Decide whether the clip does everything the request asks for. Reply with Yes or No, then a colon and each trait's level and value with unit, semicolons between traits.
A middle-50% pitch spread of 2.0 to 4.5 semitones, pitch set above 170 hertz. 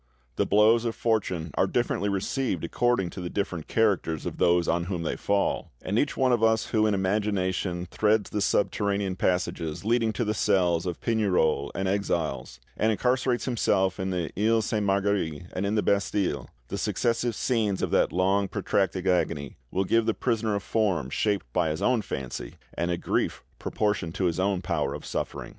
No: average, 3.7 semitones; low, 100 Hz